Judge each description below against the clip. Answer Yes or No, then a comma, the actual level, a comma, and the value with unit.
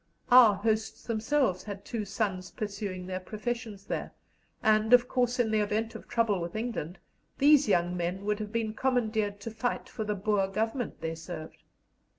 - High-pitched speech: Yes, high, 215 Hz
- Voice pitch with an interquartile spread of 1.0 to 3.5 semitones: Yes, average, 3.0 semitones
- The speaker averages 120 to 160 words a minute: No, average, 170 wpm